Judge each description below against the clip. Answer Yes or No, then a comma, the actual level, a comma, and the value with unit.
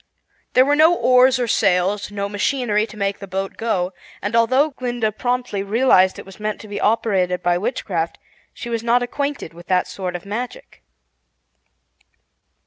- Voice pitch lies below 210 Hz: No, high, 215 Hz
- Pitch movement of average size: Yes, average, 4.2 semitones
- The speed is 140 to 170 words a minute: Yes, average, 165 wpm